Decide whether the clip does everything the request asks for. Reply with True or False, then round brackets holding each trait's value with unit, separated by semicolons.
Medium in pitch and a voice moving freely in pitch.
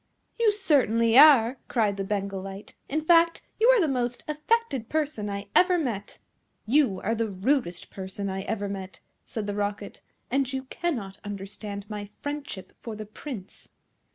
False (225 Hz; 6.4 semitones)